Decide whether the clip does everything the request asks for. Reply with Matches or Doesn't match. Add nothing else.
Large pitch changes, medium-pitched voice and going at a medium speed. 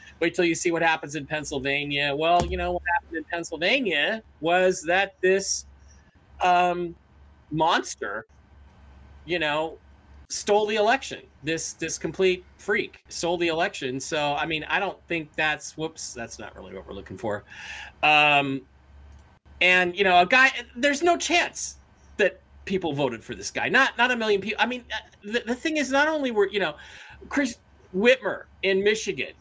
Matches